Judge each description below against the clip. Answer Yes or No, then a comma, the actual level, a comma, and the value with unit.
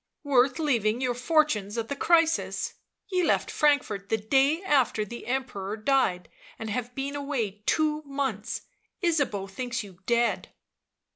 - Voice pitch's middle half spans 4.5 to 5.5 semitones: Yes, average, 5.0 semitones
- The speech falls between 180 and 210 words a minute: No, average, 145 wpm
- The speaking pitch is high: Yes, very high, 250 Hz